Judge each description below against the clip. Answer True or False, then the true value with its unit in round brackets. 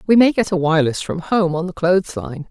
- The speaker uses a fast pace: True (265 wpm)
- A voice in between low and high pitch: True (175 Hz)